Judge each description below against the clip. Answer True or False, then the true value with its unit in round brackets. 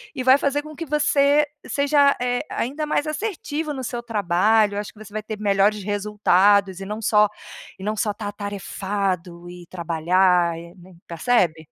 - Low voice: False (210 Hz)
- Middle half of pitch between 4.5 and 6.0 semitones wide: True (5.6 semitones)